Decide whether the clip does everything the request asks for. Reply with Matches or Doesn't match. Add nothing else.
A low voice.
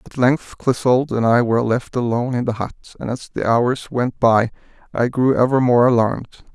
Matches